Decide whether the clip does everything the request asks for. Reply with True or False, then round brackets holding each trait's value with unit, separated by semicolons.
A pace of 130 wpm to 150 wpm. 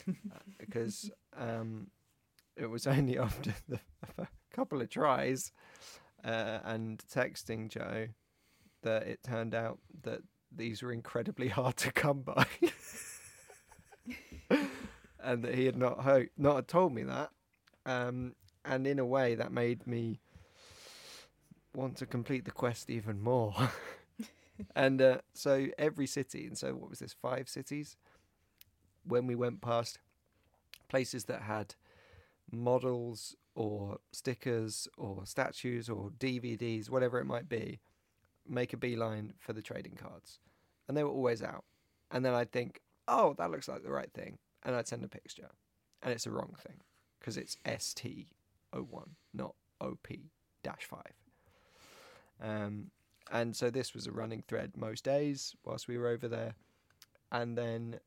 True (145 wpm)